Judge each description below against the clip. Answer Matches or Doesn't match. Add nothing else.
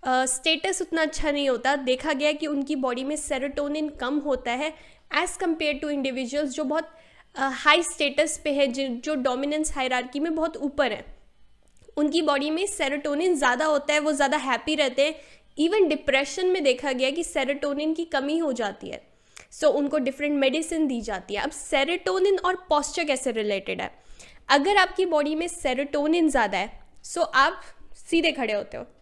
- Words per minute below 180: Doesn't match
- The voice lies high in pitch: Matches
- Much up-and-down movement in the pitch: Doesn't match